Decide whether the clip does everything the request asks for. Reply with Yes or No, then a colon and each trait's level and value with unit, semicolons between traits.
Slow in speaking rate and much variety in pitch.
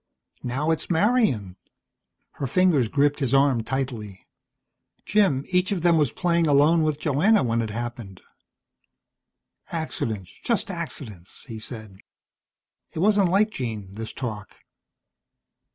Yes: slow, 120 wpm; wide, 7.1 semitones